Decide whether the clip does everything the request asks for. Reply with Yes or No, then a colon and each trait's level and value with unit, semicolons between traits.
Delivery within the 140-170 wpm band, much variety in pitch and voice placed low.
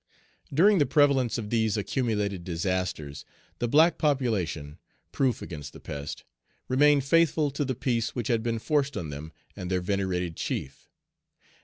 Yes: average, 150 wpm; wide, 7.5 semitones; low, 115 Hz